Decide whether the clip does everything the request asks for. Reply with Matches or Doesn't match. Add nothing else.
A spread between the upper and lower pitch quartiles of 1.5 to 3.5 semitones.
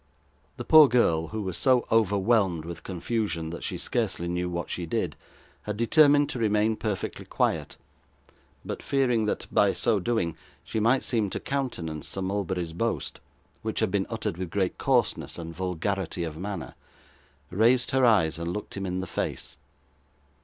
Doesn't match